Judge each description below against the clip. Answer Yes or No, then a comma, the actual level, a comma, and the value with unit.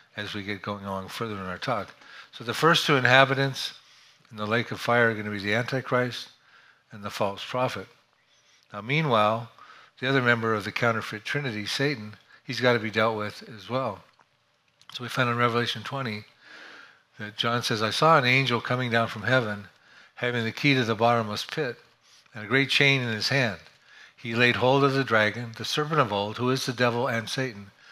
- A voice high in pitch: No, low, 120 Hz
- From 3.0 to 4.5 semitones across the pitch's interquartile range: Yes, average, 3.6 semitones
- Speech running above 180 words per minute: Yes, average, 200 wpm